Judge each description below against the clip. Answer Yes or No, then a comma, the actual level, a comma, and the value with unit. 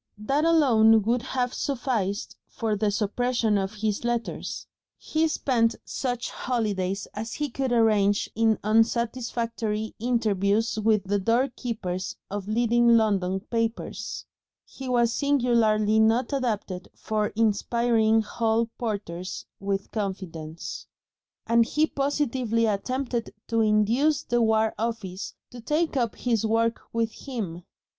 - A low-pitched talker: No, high, 225 Hz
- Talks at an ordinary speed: No, slow, 120 wpm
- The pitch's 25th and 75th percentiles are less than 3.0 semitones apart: Yes, narrow, 2.4 semitones